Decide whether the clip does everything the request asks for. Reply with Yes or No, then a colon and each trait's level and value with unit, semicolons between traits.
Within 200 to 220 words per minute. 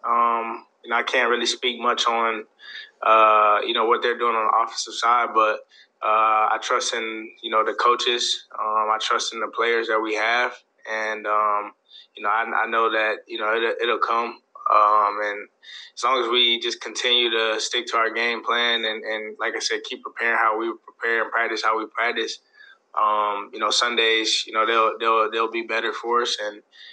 Yes: fast, 205 wpm